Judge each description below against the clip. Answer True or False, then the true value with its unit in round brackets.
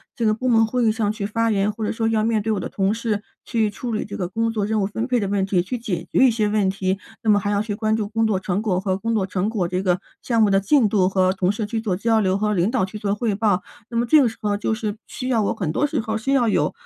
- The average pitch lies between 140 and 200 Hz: False (215 Hz)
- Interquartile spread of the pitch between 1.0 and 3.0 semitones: True (2.5 semitones)